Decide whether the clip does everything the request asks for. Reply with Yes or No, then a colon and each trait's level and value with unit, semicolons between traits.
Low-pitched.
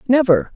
No: high, 235 Hz